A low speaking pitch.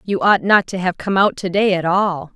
No: medium, 185 Hz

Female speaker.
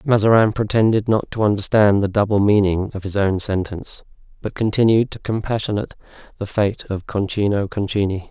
No: male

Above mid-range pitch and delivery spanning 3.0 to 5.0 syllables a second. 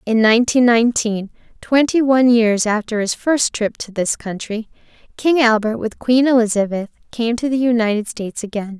No: high, 230 Hz; 5.2 syllables/s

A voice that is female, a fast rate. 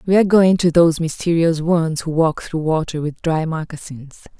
No: female; average, 190 wpm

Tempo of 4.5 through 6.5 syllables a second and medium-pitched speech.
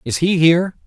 Yes: 5.6 syllables/s; medium, 160 Hz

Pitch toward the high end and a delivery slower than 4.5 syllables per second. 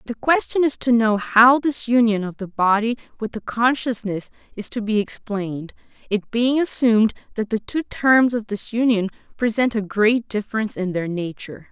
No: high, 225 Hz; 5.0 syllables/s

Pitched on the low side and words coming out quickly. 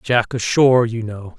No: low, 115 Hz; average, 175 wpm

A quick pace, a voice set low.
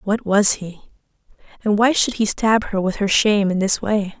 No: fast, 215 wpm; high, 205 Hz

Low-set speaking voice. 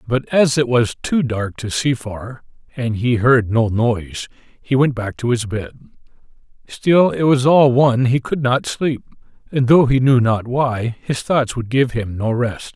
Yes: low, 125 Hz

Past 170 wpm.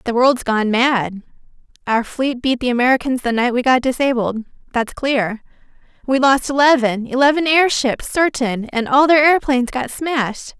No: average, 155 wpm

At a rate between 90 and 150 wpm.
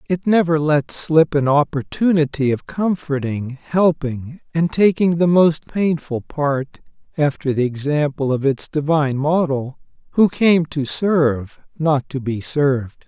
Yes: average, 140 wpm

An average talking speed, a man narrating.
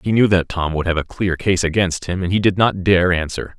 No: fast, 285 wpm; male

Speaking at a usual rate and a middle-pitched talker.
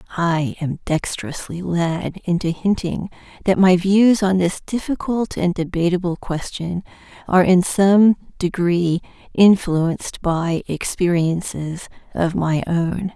No: slow, 115 wpm; medium, 180 Hz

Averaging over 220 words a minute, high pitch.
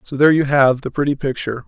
No: fast, 250 wpm; low, 135 Hz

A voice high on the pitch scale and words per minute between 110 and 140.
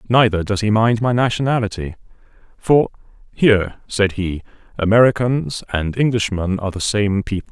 No: low, 105 Hz; slow, 135 wpm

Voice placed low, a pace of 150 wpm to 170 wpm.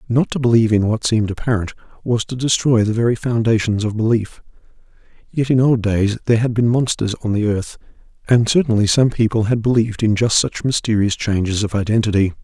No: low, 110 Hz; average, 190 wpm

